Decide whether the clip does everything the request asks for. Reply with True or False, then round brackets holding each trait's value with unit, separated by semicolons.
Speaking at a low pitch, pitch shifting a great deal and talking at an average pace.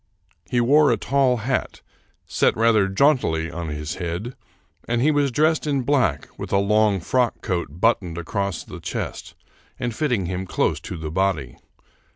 True (105 Hz; 6.8 semitones; 170 wpm)